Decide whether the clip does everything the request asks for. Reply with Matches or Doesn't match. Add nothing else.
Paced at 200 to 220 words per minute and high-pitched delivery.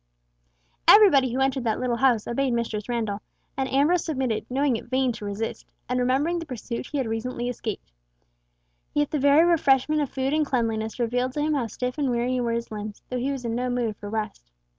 Matches